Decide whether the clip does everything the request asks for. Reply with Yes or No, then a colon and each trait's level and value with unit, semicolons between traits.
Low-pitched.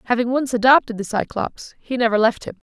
No: high, 240 Hz